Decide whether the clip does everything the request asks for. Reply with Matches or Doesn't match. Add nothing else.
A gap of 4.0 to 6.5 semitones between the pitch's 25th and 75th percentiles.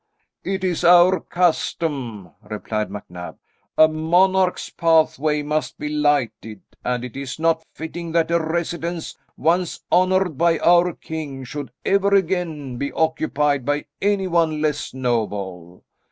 Matches